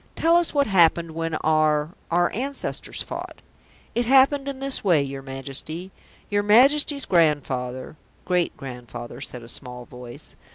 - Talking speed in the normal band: Yes, average, 150 wpm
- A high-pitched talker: No, medium, 165 Hz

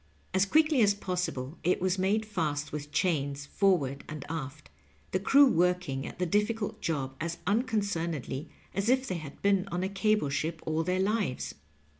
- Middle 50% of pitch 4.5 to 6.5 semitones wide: Yes, average, 5.0 semitones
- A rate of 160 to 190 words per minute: Yes, average, 170 wpm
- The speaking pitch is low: No, medium, 180 Hz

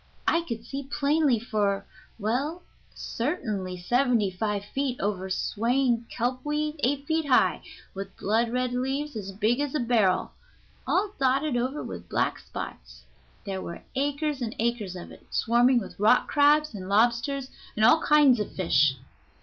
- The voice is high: Yes, high, 240 Hz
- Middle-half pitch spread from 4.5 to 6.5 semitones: Yes, average, 5.3 semitones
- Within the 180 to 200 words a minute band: No, average, 155 wpm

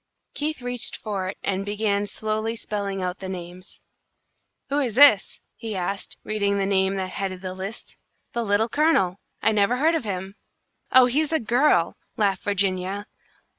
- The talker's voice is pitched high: Yes, high, 205 Hz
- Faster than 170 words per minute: No, average, 165 wpm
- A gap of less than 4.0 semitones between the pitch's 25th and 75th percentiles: Yes, average, 3.4 semitones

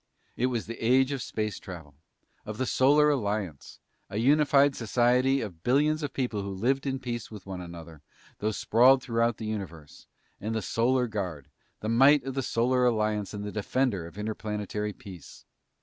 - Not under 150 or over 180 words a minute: Yes, average, 175 wpm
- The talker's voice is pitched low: Yes, low, 115 Hz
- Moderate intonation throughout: Yes, average, 4.1 semitones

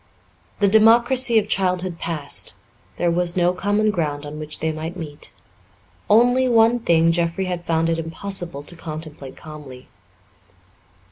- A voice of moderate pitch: Yes, medium, 170 Hz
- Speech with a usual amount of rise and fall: Yes, average, 4.4 semitones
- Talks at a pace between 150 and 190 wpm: No, average, 140 wpm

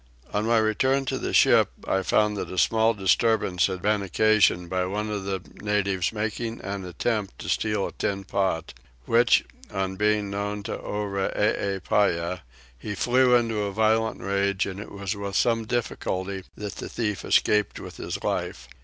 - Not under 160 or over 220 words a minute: Yes, average, 170 wpm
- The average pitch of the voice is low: Yes, low, 105 Hz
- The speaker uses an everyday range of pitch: No, narrow, 2.2 semitones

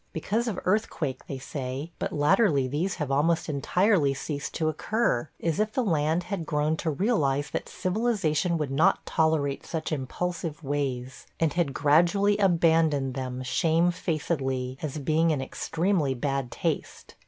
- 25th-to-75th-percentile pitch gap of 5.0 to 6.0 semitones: No, average, 4.1 semitones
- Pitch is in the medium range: Yes, medium, 155 Hz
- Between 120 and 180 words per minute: Yes, average, 145 wpm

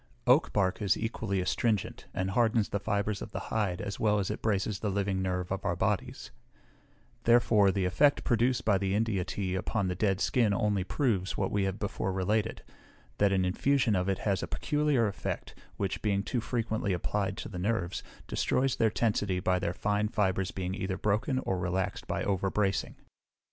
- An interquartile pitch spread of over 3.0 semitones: No, average, 2.7 semitones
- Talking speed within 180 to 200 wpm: Yes, average, 185 wpm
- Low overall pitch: Yes, low, 100 Hz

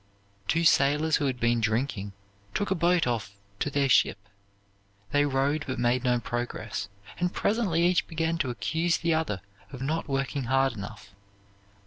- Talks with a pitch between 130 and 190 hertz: Yes, low, 135 Hz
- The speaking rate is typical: Yes, average, 160 wpm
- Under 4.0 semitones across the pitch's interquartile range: No, average, 5.2 semitones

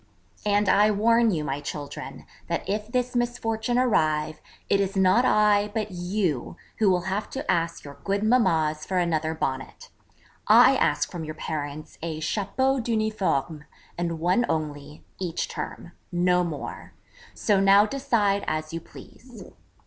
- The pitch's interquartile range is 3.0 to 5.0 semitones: No, wide, 5.4 semitones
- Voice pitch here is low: No, high, 190 Hz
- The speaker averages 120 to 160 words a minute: Yes, average, 150 wpm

